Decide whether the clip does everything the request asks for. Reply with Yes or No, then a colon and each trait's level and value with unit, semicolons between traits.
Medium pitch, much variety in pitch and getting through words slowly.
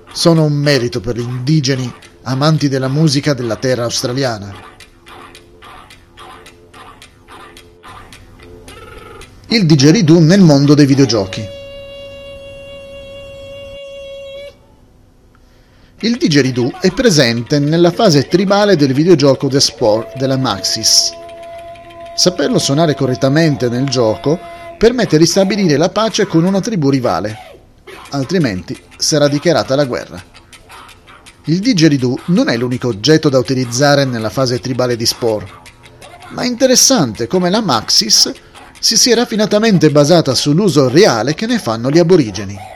Yes: medium, 145 Hz; wide, 8.6 semitones; slow, 110 wpm